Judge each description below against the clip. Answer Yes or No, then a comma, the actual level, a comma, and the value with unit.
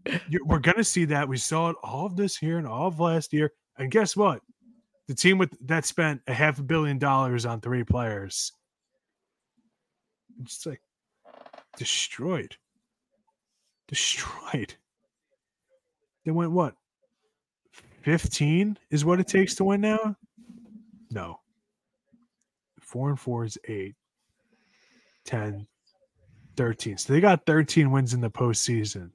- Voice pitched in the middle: Yes, medium, 160 Hz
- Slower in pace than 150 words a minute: Yes, slow, 135 wpm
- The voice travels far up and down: Yes, wide, 8.8 semitones